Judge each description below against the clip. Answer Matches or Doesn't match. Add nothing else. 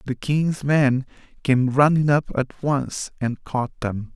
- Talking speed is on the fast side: Doesn't match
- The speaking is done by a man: Matches